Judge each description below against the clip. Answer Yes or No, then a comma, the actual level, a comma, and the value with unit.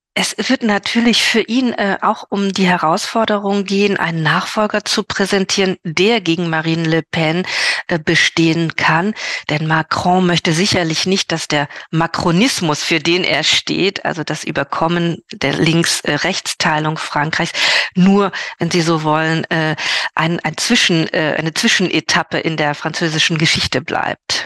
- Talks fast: No, average, 140 wpm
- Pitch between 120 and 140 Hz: No, medium, 170 Hz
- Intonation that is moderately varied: Yes, average, 3.6 semitones